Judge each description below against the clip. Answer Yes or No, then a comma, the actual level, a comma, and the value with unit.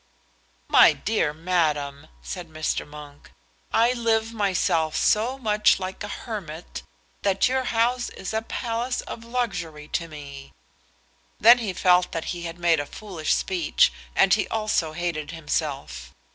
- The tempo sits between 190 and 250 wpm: No, average, 145 wpm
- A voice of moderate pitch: Yes, medium, 180 Hz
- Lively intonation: Yes, wide, 6.3 semitones